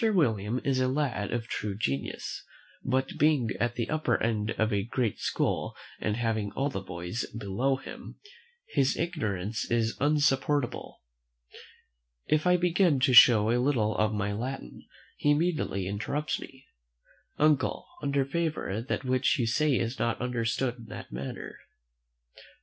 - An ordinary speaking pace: Yes, average, 145 wpm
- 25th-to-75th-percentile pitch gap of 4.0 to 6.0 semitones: Yes, average, 4.8 semitones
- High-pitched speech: No, low, 120 Hz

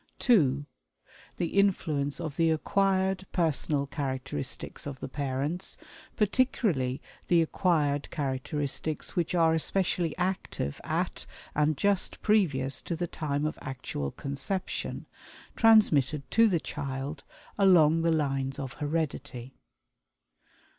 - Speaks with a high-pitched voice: No, medium, 155 Hz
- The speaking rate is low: Yes, slow, 110 wpm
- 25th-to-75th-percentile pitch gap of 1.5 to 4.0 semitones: No, average, 4.6 semitones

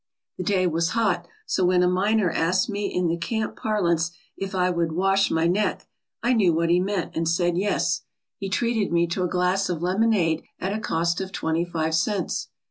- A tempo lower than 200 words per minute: No, fast, 205 wpm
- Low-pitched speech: No, medium, 180 Hz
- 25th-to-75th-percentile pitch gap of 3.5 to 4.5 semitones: No, average, 2.8 semitones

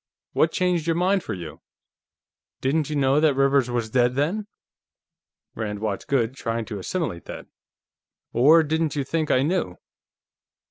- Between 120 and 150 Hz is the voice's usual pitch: Yes, medium, 140 Hz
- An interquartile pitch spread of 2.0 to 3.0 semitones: No, wide, 5.6 semitones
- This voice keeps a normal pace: Yes, average, 150 wpm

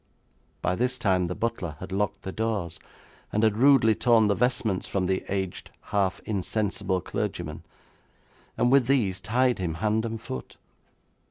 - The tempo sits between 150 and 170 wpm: Yes, average, 155 wpm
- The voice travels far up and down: No, average, 3.6 semitones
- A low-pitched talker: Yes, low, 105 Hz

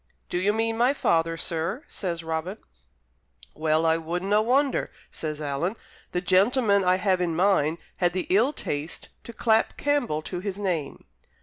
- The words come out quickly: No, average, 165 wpm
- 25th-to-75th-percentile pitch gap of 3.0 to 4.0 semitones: No, average, 5.0 semitones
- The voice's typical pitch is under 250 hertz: Yes, medium, 185 Hz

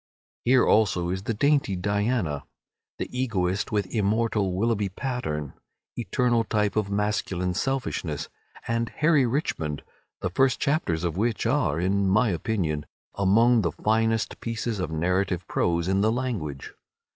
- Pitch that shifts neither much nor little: Yes, average, 4.6 semitones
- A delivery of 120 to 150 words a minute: Yes, slow, 135 wpm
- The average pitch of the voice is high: No, low, 105 Hz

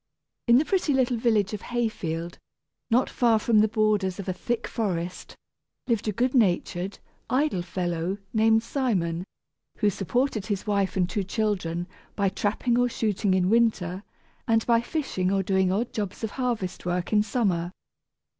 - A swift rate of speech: No, average, 165 wpm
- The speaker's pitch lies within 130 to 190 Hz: No, high, 210 Hz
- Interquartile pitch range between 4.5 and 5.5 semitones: No, average, 4.1 semitones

